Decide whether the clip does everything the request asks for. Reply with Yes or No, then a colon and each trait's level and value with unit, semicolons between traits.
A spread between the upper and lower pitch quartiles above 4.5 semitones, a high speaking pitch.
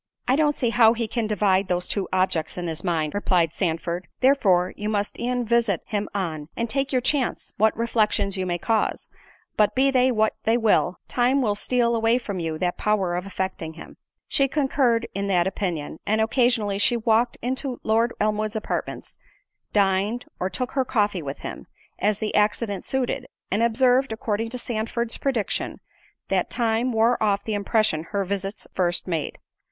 No: average, 3.9 semitones; high, 215 Hz